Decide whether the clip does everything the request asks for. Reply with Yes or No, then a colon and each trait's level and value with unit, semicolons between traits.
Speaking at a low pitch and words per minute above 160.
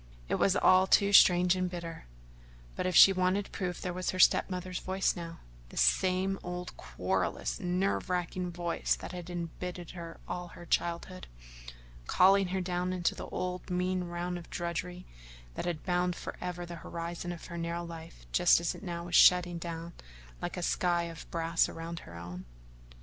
No: medium, 175 Hz; average, 175 wpm